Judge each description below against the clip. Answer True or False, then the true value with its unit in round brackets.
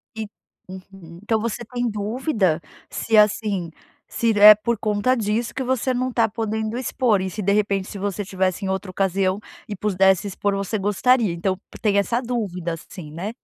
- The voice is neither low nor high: False (205 Hz)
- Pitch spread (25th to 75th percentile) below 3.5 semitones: True (3.0 semitones)